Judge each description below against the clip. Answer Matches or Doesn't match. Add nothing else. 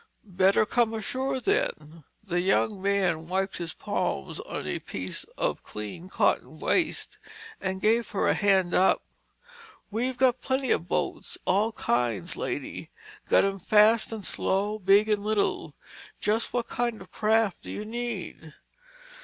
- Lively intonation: Doesn't match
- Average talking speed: Matches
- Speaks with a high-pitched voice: Matches